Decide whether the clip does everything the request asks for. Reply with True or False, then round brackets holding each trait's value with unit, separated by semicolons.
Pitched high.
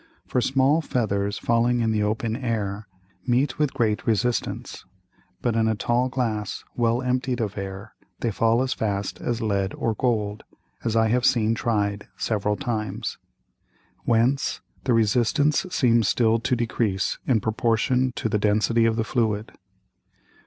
False (115 Hz)